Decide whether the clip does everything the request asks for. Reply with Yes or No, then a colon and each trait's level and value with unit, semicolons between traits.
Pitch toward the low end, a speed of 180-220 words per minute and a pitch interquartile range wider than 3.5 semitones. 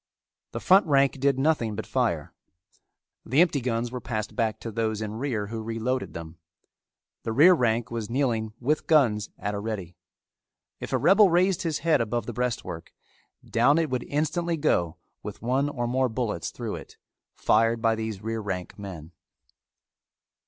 No: low, 115 Hz; average, 165 wpm; average, 4.3 semitones